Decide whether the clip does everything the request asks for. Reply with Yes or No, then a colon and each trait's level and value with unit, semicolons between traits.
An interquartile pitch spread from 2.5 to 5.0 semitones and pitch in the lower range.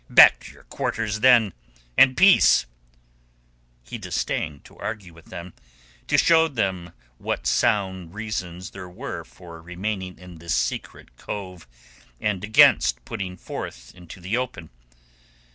Yes: average, 3.9 semitones; very low, 95 Hz